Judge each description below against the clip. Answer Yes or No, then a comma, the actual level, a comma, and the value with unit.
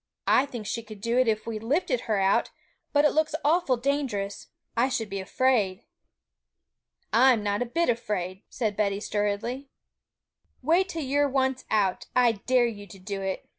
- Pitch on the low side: No, high, 230 Hz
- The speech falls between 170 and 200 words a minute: Yes, average, 175 wpm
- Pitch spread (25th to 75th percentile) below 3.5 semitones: No, average, 4.5 semitones